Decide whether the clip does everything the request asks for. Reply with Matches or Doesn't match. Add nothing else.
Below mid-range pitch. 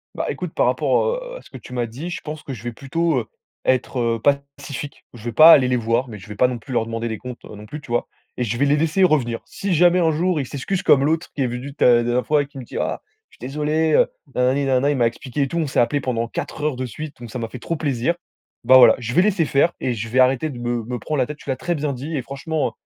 Matches